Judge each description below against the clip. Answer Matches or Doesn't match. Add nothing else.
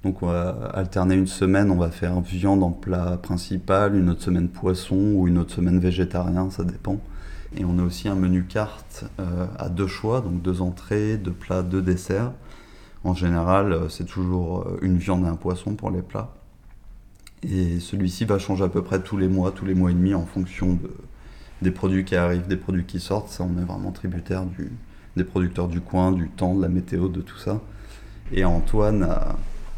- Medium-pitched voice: Doesn't match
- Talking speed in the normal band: Matches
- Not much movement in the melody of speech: Matches